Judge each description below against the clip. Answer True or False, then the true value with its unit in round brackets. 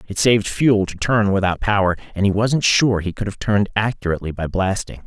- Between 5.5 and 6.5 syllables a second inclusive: True (5.8 syllables/s)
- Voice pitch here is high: False (100 Hz)